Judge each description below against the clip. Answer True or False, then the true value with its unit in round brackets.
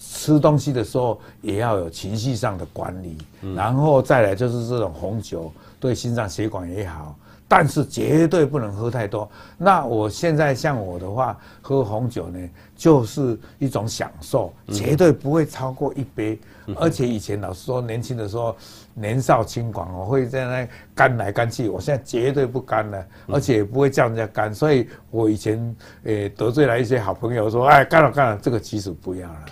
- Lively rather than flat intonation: False (4.5 semitones)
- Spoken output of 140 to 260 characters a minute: False (270 characters per minute)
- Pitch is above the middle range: False (115 Hz)